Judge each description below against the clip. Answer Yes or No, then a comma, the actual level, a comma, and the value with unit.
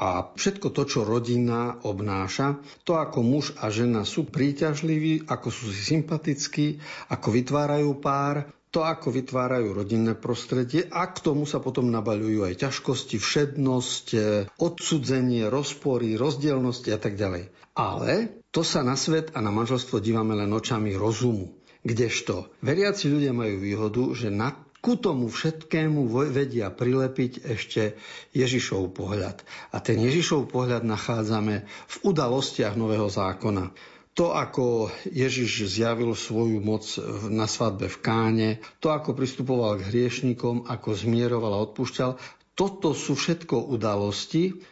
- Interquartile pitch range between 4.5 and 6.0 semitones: Yes, average, 4.8 semitones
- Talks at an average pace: Yes, average, 135 wpm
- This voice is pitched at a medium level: No, low, 125 Hz